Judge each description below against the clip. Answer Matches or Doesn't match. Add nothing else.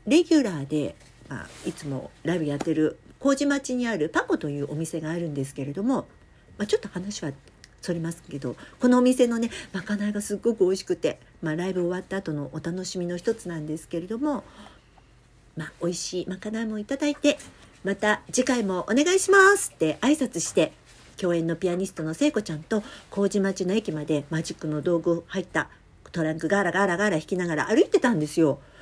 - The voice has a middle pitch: Matches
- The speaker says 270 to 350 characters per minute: Doesn't match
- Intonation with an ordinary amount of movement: Doesn't match